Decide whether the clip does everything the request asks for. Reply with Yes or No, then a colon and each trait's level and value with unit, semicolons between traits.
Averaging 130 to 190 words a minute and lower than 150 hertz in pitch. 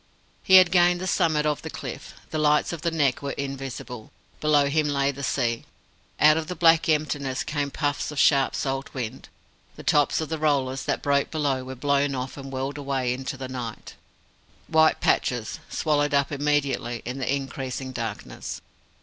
Yes: average, 180 wpm; medium, 140 Hz